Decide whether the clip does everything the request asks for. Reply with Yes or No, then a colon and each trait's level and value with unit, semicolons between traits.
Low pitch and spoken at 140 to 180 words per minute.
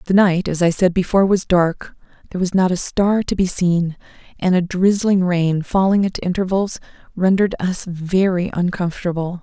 No: medium, 185 Hz; average, 170 wpm